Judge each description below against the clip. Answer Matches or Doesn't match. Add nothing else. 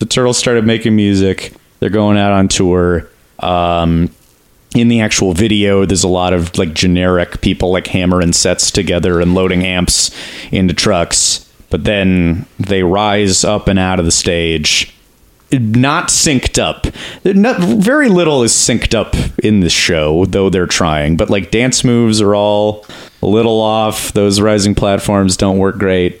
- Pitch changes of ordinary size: Matches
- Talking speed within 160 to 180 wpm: Matches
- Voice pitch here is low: Matches